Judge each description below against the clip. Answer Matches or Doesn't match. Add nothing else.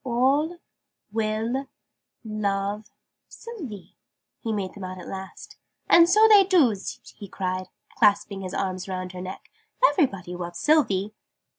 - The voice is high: Matches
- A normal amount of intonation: Doesn't match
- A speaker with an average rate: Doesn't match